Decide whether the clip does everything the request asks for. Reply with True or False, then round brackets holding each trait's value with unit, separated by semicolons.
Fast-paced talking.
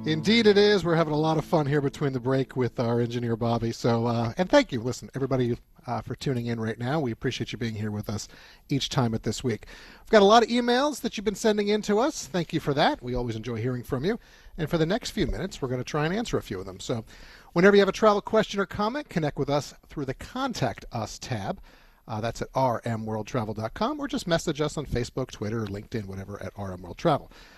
True (250 wpm)